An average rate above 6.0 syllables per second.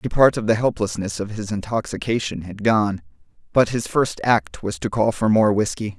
No: 5.0 syllables/s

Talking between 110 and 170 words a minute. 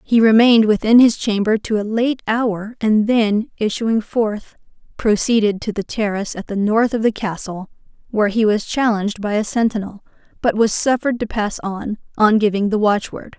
No: average, 185 wpm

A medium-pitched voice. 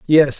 Yes: medium, 150 Hz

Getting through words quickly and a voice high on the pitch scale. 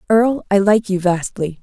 No: average, 185 wpm; high, 200 Hz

